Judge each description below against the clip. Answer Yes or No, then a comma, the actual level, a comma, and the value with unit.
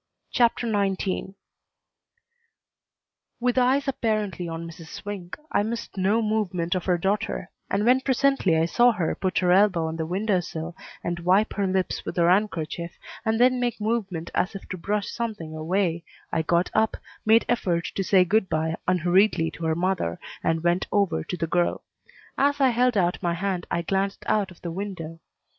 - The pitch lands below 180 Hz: No, high, 190 Hz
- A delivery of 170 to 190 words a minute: Yes, average, 180 wpm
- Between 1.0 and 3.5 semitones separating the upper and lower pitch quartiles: No, average, 4.0 semitones